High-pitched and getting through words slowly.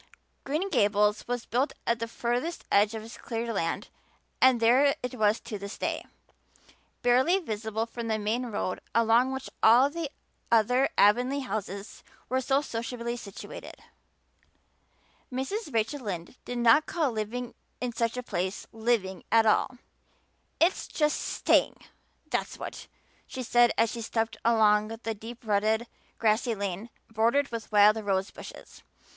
No: high, 230 Hz; average, 145 wpm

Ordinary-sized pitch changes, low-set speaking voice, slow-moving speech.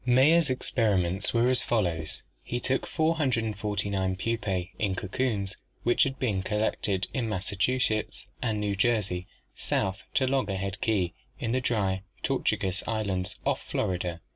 Yes: average, 4.4 semitones; low, 105 Hz; slow, 130 wpm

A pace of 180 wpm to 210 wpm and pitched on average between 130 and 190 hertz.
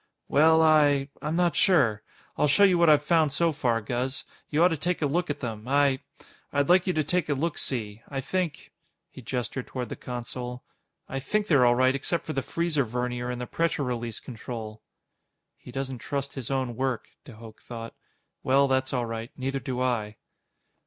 Yes: average, 200 wpm; low, 135 Hz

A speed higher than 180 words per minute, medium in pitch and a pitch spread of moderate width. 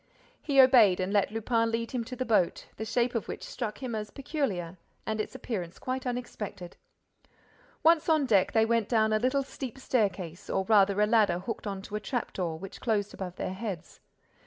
No: average, 200 wpm; high, 220 Hz; average, 4.2 semitones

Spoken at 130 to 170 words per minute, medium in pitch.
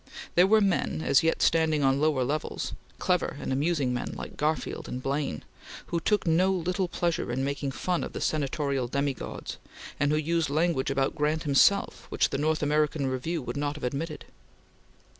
No: average, 180 wpm; medium, 150 Hz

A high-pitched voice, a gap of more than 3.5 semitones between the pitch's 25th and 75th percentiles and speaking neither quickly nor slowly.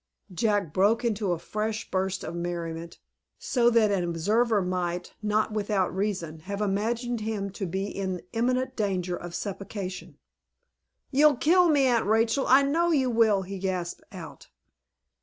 Yes: high, 205 Hz; average, 4.1 semitones; average, 150 wpm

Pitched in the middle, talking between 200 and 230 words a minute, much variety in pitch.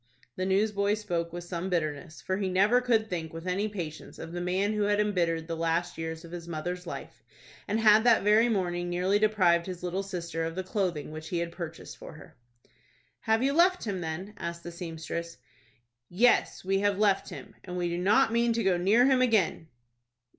No: medium, 180 Hz; fast, 205 wpm; average, 3.6 semitones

